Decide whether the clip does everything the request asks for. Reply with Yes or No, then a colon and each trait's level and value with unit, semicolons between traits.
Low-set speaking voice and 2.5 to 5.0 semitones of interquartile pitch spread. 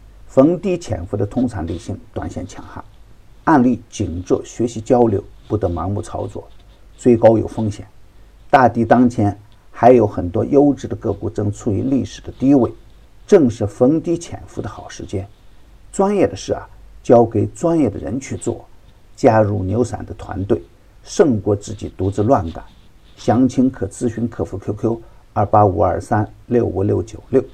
Yes: low, 105 Hz; average, 3.2 semitones